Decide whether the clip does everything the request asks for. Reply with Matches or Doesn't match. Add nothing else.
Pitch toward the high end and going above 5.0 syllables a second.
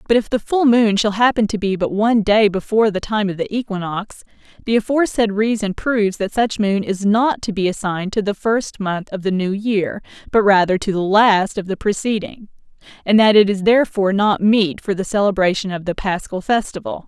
Matches